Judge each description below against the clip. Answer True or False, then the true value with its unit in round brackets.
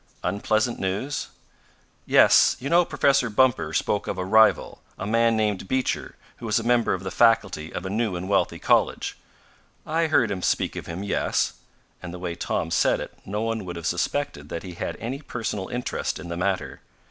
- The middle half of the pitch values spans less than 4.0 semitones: False (4.5 semitones)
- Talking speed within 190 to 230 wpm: True (195 wpm)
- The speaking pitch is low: True (105 Hz)